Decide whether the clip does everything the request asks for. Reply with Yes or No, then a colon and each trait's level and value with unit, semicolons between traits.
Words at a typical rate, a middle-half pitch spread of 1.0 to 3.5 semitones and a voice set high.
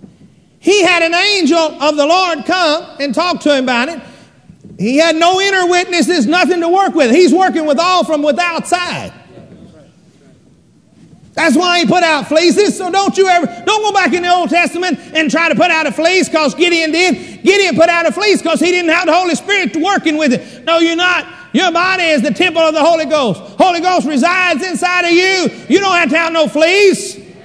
No: fast, 210 wpm; average, 2.8 semitones; very high, 335 Hz